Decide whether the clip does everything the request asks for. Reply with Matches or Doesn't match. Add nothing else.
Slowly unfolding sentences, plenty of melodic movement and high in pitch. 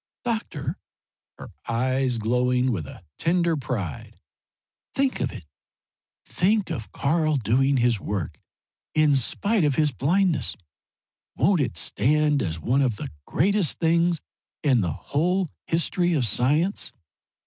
Doesn't match